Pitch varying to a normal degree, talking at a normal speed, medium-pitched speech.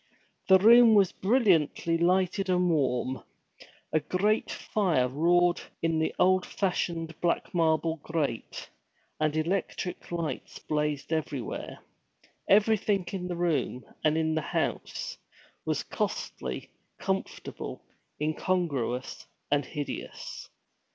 No: average, 3.6 semitones; slow, 105 wpm; medium, 165 Hz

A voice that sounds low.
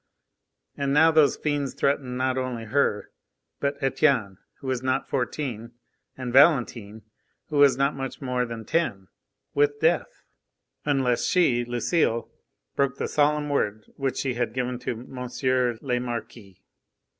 Yes: low, 130 Hz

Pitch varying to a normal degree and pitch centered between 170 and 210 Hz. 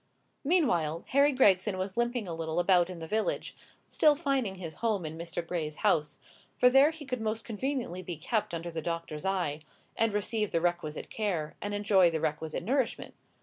No: wide, 5.8 semitones; high, 190 Hz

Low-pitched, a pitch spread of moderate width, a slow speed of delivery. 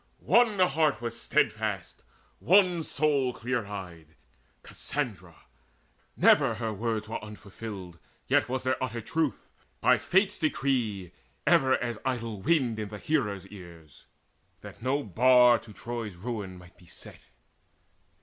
Yes: low, 115 Hz; average, 4.7 semitones; slow, 130 wpm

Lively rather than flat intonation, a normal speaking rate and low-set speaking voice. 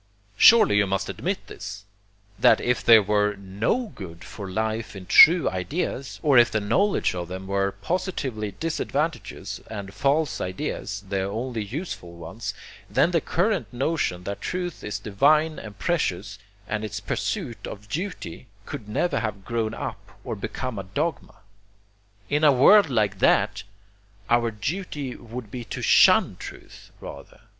Yes: wide, 6.9 semitones; average, 150 wpm; low, 110 Hz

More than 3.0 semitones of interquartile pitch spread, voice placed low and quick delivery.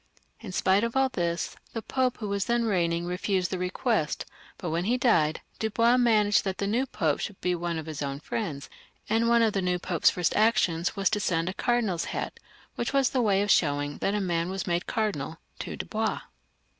No: average, 4.9 semitones; high, 195 Hz; fast, 210 wpm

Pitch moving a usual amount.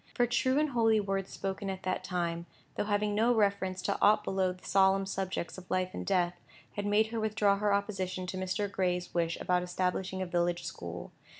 No: narrow, 2.2 semitones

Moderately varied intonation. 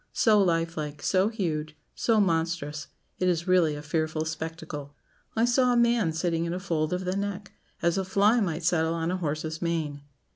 Yes: average, 3.3 semitones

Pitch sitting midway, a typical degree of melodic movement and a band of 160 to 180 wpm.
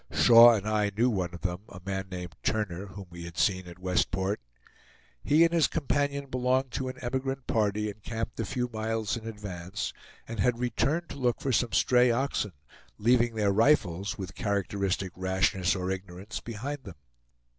No: low, 105 Hz; average, 4.6 semitones; average, 175 wpm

